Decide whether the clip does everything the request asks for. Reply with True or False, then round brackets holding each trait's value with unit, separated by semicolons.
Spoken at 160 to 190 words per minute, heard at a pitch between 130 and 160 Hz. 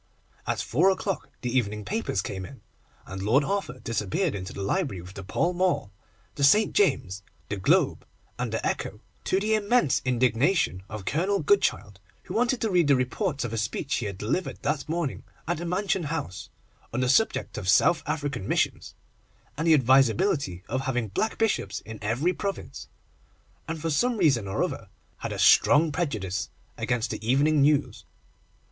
True (175 wpm; 140 Hz)